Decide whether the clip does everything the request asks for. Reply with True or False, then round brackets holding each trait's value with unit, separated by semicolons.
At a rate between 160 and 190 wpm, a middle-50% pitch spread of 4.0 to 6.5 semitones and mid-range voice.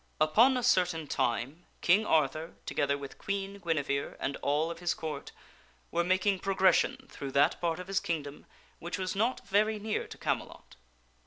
True (165 wpm; 4.9 semitones; 170 Hz)